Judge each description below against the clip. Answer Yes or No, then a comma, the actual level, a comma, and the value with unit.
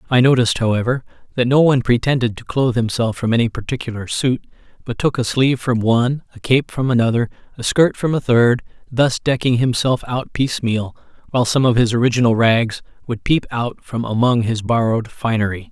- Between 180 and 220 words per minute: Yes, average, 185 wpm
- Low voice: Yes, low, 120 Hz